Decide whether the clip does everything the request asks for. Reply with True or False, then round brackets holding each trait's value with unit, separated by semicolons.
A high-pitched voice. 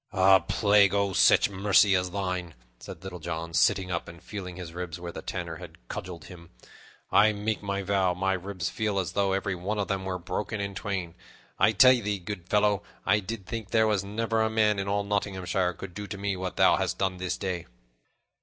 False (95 Hz)